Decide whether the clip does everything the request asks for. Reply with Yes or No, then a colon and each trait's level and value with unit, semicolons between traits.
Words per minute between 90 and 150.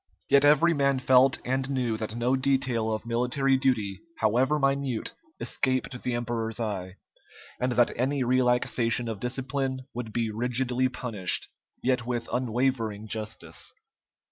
Yes: slow, 135 wpm